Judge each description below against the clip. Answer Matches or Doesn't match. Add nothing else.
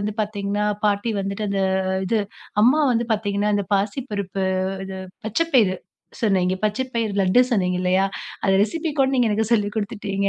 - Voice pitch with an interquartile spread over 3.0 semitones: Doesn't match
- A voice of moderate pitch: Doesn't match